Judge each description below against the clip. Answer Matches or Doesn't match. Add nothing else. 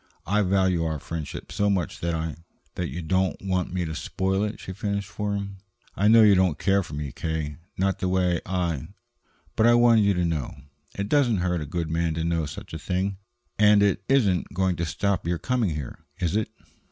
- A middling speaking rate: Doesn't match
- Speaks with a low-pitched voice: Matches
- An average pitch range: Matches